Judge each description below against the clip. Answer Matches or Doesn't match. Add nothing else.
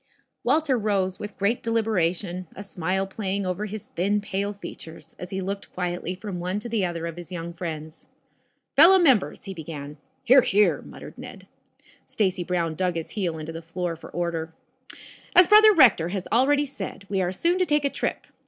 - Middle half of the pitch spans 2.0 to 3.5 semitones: Doesn't match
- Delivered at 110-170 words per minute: Doesn't match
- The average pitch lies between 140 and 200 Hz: Matches